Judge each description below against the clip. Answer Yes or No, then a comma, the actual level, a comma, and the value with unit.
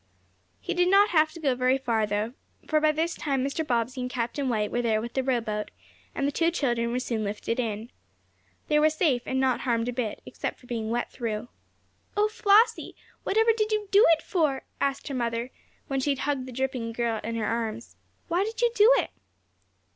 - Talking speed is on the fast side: Yes, fast, 215 wpm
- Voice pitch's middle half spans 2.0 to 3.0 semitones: No, average, 5.1 semitones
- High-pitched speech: Yes, very high, 255 Hz